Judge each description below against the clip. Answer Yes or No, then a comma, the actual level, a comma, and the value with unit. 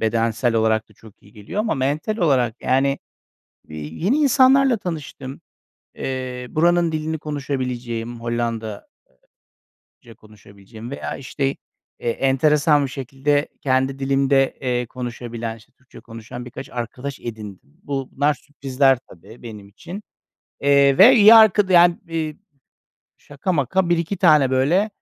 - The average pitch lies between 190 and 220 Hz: No, low, 135 Hz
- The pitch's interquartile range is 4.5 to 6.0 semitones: Yes, average, 4.8 semitones